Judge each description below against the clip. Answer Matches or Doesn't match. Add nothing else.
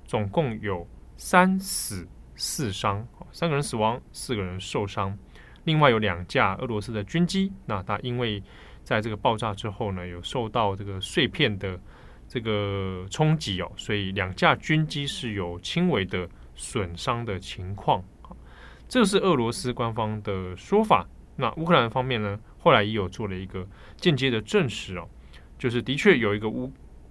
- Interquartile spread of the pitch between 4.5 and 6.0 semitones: Matches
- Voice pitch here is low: Matches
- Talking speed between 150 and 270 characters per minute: Matches